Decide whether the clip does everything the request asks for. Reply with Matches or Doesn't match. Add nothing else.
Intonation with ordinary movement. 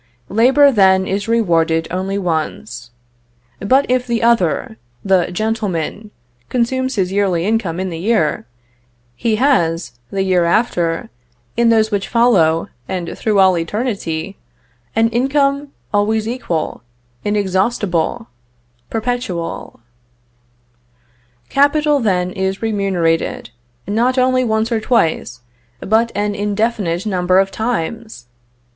Matches